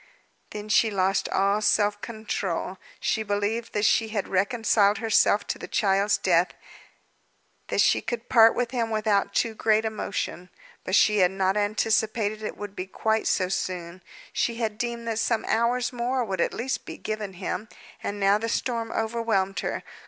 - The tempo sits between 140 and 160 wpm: No, average, 170 wpm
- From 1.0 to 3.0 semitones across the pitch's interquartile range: Yes, narrow, 2.4 semitones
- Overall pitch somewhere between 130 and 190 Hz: No, high, 215 Hz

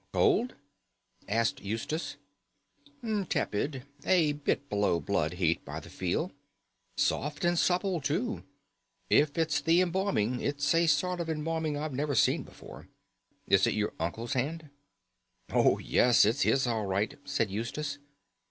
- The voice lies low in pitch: No, medium, 145 Hz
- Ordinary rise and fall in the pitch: No, wide, 6.3 semitones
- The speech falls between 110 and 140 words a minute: Yes, slow, 135 wpm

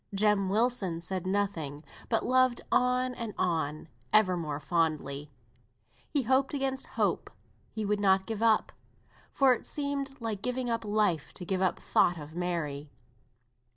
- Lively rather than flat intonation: Yes, wide, 6.5 semitones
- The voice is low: No, high, 205 Hz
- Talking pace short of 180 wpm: Yes, average, 150 wpm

